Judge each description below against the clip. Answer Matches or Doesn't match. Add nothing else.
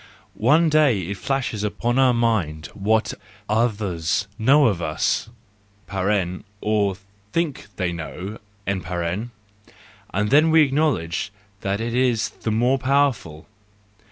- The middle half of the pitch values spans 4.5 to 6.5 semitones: Matches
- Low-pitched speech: Matches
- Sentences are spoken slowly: Matches